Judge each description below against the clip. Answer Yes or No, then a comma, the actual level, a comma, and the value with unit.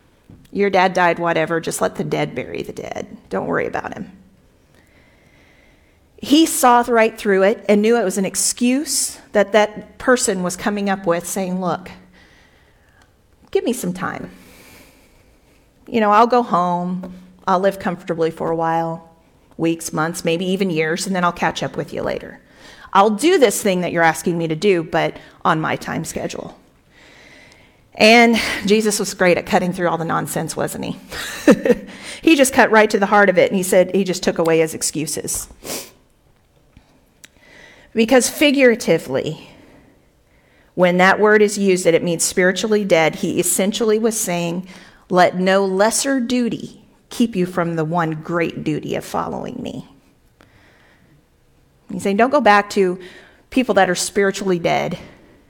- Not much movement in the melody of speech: No, average, 4.2 semitones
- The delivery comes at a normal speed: Yes, average, 160 wpm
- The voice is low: No, high, 190 Hz